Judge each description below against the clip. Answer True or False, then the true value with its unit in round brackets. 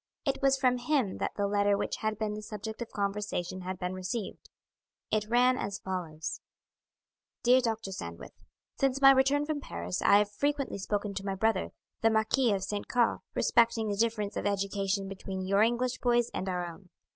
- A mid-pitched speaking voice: False (210 Hz)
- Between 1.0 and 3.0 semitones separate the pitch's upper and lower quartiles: False (3.8 semitones)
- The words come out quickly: False (185 wpm)